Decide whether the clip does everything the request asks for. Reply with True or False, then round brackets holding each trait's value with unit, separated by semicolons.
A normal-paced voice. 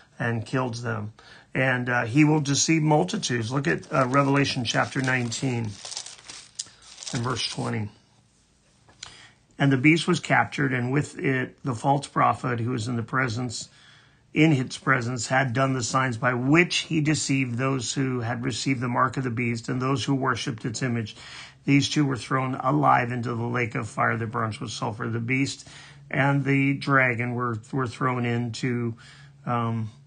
True (170 wpm)